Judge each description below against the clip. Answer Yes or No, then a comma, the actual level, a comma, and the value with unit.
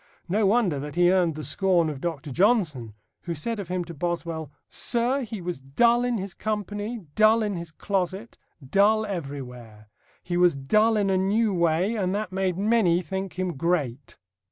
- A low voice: No, medium, 185 Hz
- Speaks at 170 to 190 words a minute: Yes, average, 180 wpm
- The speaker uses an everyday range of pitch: Yes, average, 4.7 semitones